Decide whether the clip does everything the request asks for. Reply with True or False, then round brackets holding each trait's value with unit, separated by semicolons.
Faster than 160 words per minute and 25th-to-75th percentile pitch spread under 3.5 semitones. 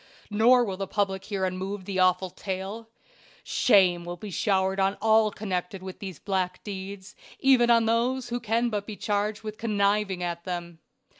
True (170 wpm; 2.6 semitones)